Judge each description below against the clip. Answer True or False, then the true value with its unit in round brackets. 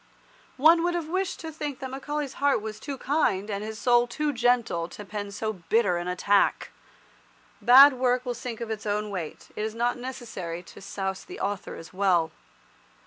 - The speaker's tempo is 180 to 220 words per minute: True (190 wpm)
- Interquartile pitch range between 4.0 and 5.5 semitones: True (5.1 semitones)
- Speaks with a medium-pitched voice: False (230 Hz)